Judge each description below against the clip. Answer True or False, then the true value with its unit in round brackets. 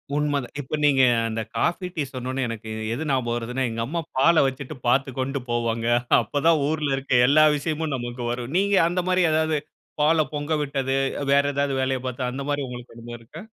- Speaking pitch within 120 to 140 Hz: True (135 Hz)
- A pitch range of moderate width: True (3.6 semitones)